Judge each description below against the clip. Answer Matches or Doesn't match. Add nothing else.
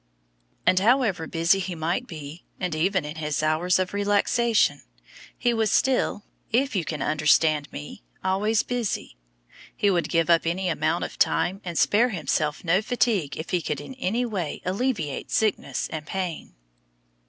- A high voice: Doesn't match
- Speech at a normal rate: Matches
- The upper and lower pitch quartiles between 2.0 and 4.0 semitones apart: Doesn't match